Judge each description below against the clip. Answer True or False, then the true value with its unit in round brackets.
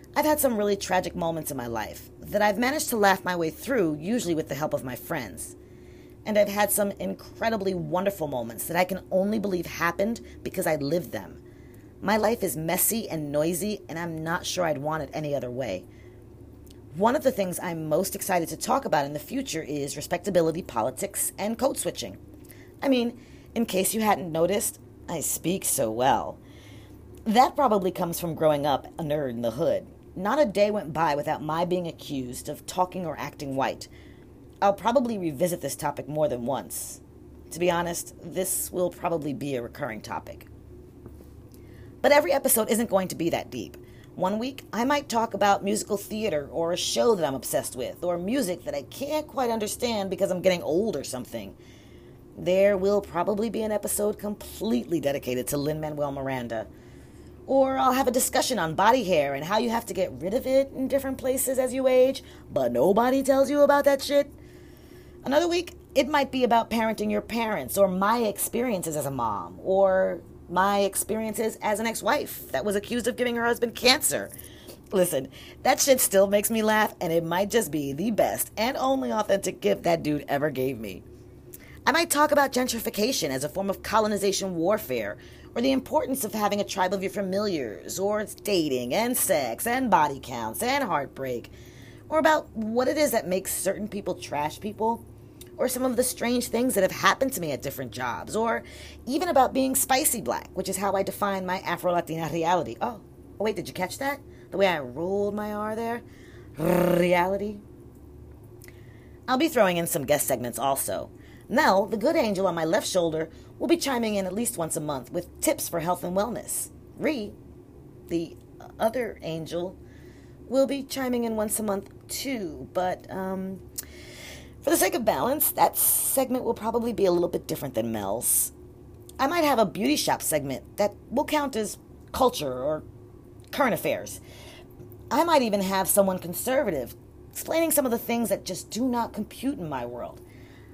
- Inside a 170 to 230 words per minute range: True (190 wpm)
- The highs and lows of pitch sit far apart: True (6.2 semitones)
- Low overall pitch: False (200 Hz)